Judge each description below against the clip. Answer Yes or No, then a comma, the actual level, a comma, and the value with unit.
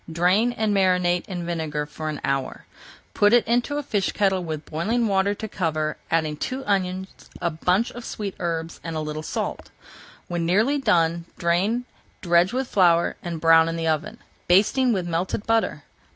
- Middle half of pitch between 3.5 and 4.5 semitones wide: Yes, average, 4.2 semitones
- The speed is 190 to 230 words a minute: No, average, 175 wpm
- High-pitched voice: No, medium, 180 Hz